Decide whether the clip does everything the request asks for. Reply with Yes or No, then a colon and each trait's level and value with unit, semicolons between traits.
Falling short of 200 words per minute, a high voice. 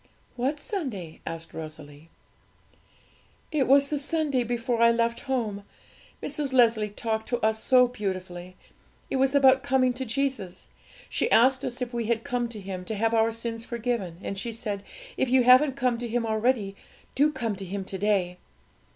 Yes: average, 175 wpm; high, 235 Hz